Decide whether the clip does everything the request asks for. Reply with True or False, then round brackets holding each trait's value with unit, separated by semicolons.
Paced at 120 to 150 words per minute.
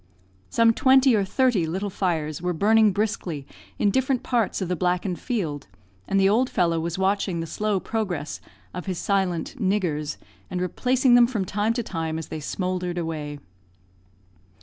False (165 wpm)